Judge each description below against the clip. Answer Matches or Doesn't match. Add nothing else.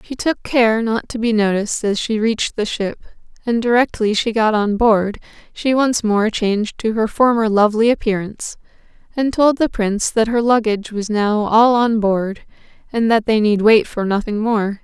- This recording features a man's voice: Doesn't match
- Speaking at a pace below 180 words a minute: Doesn't match